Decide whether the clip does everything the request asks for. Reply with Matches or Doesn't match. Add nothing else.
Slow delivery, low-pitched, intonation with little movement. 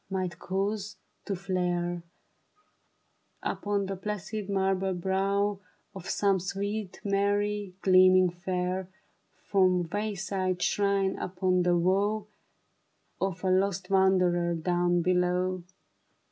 Doesn't match